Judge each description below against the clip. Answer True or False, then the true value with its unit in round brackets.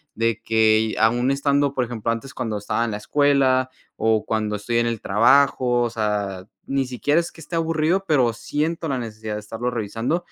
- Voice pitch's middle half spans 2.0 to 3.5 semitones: False (4.1 semitones)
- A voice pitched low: True (120 Hz)